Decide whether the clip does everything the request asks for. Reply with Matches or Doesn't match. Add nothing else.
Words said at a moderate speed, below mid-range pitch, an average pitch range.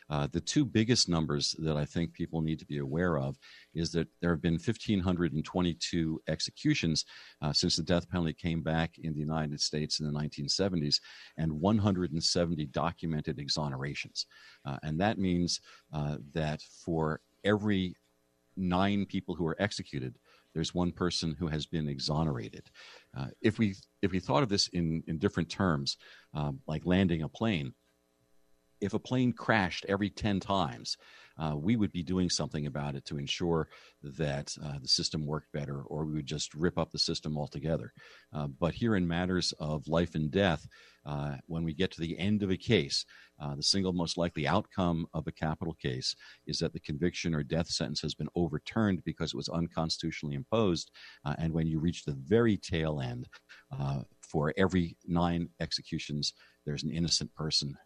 Matches